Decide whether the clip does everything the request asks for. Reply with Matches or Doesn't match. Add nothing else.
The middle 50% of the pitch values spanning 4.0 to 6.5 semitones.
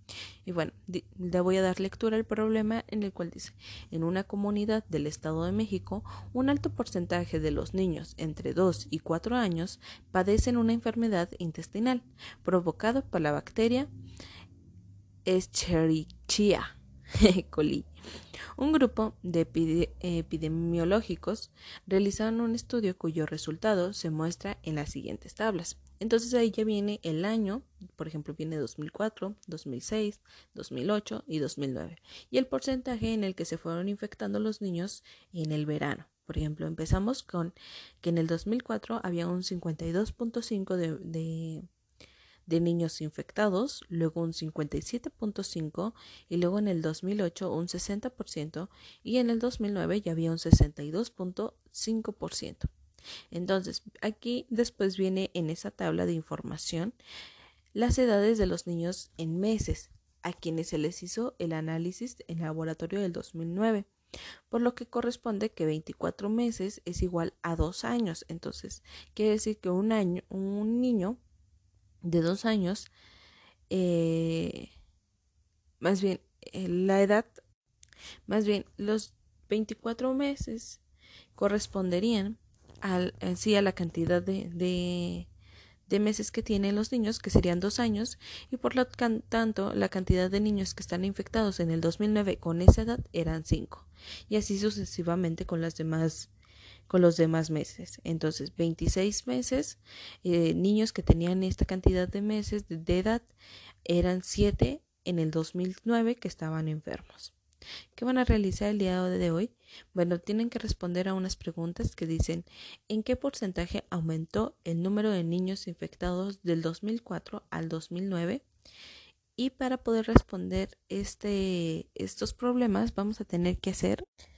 Matches